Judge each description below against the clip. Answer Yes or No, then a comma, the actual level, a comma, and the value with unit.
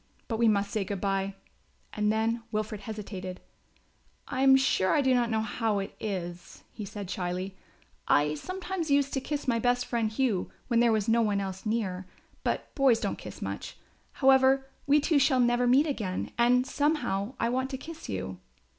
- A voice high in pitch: Yes, high, 225 Hz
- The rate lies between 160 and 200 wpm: Yes, average, 185 wpm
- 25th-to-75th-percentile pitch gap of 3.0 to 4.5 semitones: No, average, 5.0 semitones